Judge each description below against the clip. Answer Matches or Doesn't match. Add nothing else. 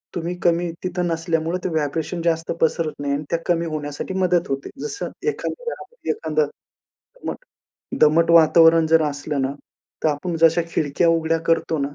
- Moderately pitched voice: Matches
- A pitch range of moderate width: Doesn't match